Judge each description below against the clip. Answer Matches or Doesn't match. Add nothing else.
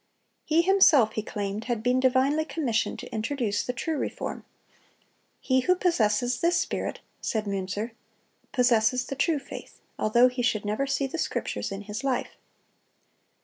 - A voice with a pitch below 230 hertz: Doesn't match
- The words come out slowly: Doesn't match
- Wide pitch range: Doesn't match